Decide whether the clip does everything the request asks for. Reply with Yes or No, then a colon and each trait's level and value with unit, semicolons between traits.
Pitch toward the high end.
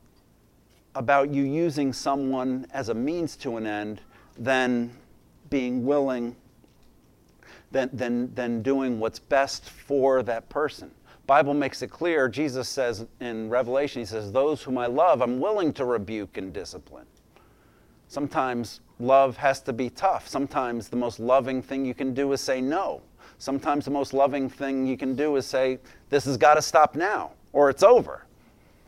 No: low, 130 Hz